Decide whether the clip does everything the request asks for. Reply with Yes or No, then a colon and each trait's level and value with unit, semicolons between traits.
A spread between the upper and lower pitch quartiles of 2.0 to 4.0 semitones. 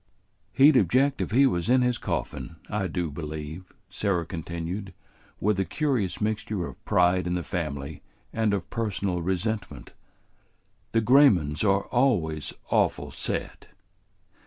No: average, 4.7 semitones